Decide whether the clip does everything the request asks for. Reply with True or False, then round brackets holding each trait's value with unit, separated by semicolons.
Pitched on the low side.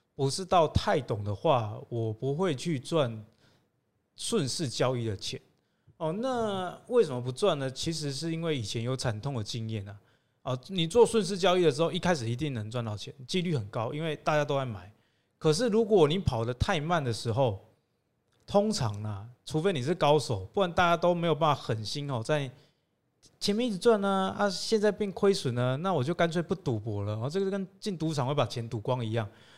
False (145 Hz)